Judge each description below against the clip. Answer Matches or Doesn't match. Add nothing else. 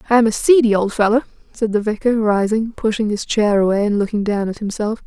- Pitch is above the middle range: Matches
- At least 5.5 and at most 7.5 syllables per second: Matches